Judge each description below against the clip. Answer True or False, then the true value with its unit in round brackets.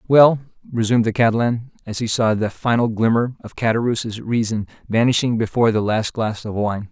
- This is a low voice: True (115 Hz)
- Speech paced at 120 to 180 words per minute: True (175 wpm)